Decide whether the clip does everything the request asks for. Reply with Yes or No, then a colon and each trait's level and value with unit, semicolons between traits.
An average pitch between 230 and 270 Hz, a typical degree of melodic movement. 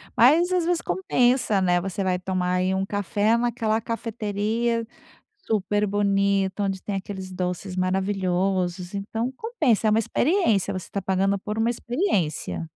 No: high, 200 Hz; average, 3.4 semitones